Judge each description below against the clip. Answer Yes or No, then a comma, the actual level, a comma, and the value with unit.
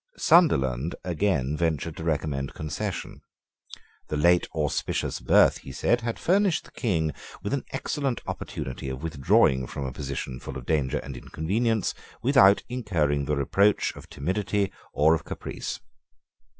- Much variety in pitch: Yes, wide, 6.8 semitones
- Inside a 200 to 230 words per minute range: No, average, 140 wpm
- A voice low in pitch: Yes, very low, 80 Hz